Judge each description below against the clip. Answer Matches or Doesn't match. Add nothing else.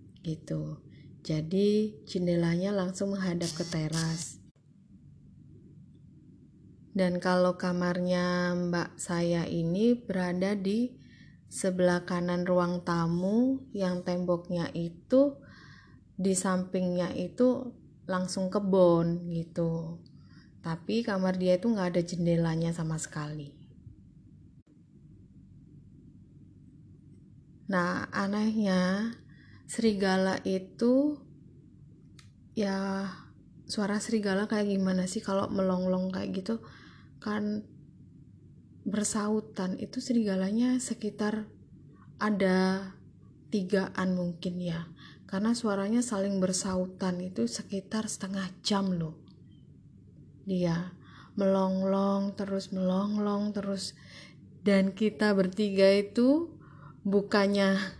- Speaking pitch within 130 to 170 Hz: Doesn't match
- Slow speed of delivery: Matches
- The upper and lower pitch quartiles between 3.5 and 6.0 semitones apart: Doesn't match